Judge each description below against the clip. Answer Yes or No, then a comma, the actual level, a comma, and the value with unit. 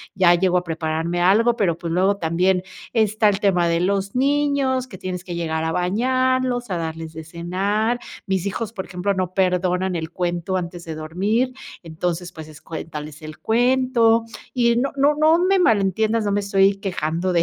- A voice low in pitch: No, high, 190 Hz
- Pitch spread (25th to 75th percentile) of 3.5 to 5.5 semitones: Yes, average, 4.9 semitones